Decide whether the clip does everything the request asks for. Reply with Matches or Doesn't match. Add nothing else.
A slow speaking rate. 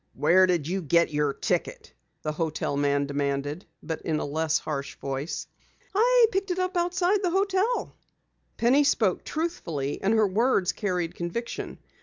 Doesn't match